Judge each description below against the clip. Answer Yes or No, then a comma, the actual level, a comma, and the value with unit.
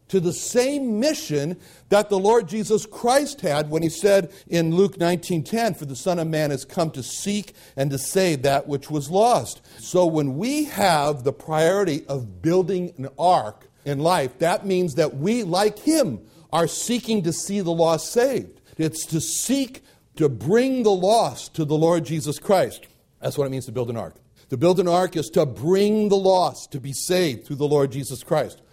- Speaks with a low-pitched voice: No, medium, 170 Hz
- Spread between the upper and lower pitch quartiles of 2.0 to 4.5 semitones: No, average, 5.1 semitones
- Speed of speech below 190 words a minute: No, average, 195 wpm